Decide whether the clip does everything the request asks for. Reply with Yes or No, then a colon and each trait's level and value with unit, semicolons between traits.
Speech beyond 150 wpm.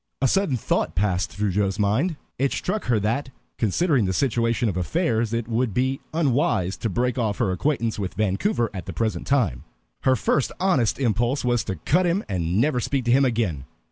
Yes: average, 195 wpm